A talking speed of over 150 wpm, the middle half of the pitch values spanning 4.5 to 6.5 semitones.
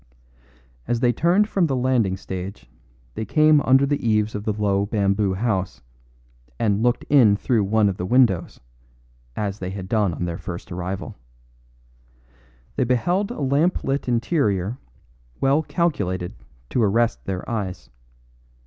No: average, 145 wpm; average, 5.2 semitones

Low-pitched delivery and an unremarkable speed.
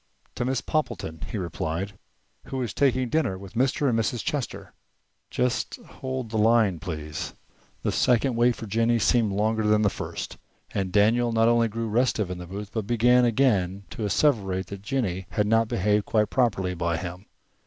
Yes: low, 110 Hz; average, 175 wpm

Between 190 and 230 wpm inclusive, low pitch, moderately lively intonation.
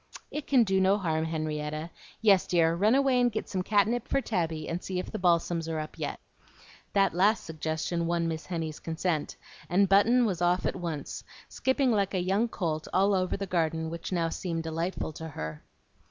No: average, 195 wpm; medium, 175 Hz; average, 3.6 semitones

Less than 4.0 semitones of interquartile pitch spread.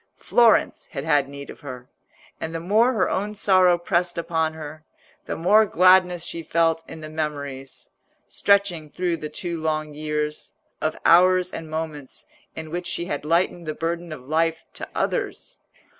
Yes: narrow, 2.5 semitones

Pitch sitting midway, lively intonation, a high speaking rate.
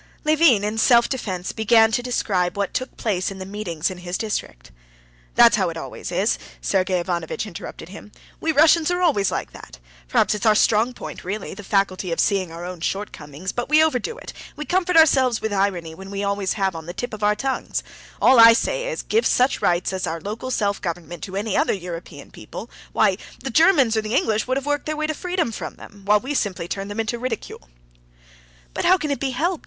No: high, 210 Hz; wide, 5.7 semitones; fast, 215 wpm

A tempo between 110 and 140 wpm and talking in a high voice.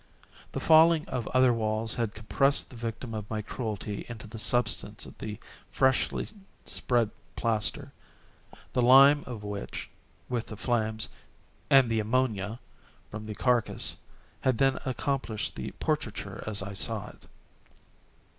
No: slow, 135 wpm; low, 115 Hz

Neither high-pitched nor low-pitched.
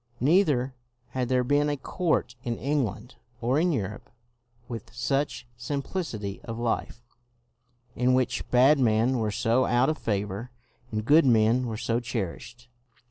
No: low, 125 Hz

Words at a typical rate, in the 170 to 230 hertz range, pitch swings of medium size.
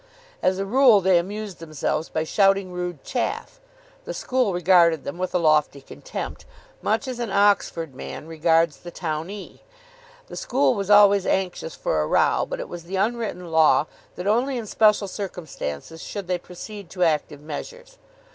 Yes: average, 165 wpm; medium, 185 Hz; average, 4.2 semitones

